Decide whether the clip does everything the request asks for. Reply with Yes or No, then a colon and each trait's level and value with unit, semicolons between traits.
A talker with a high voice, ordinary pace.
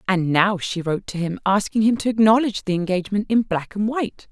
No: high, 200 Hz; fast, 220 wpm